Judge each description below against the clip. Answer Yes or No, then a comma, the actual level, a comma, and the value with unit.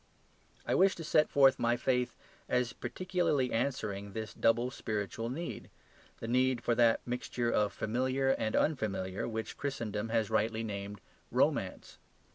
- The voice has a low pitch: Yes, low, 120 Hz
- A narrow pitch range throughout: No, average, 3.1 semitones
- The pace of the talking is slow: No, average, 150 wpm